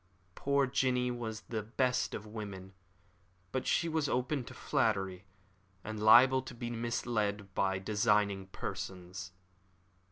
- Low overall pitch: Yes, low, 110 Hz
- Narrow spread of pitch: No, average, 4.0 semitones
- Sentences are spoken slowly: Yes, slow, 125 wpm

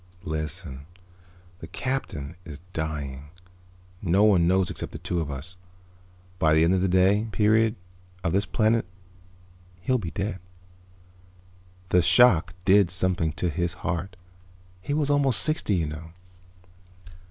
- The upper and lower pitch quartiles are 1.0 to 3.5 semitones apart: No, average, 4.3 semitones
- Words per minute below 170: Yes, slow, 135 wpm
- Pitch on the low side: Yes, very low, 90 Hz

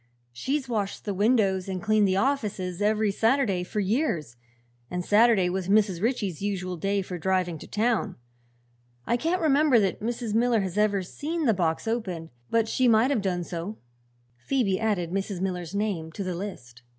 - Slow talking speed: No, average, 175 wpm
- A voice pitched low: No, high, 200 Hz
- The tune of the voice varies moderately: Yes, average, 3.8 semitones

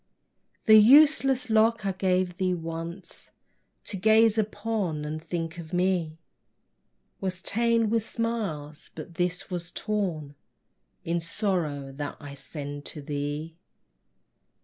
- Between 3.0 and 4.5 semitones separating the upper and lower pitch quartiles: No, wide, 5.5 semitones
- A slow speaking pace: Yes, slow, 120 wpm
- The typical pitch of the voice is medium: Yes, medium, 180 Hz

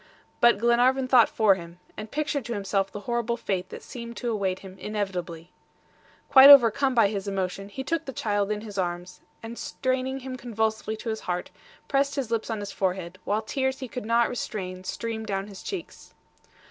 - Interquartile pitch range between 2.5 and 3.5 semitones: No, average, 4.3 semitones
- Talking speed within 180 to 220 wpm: Yes, average, 190 wpm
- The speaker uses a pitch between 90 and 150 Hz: No, high, 220 Hz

